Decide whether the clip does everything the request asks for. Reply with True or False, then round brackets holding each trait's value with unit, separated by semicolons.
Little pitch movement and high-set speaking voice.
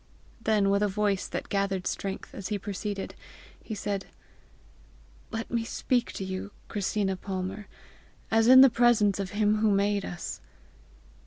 True (1.9 semitones; 205 Hz)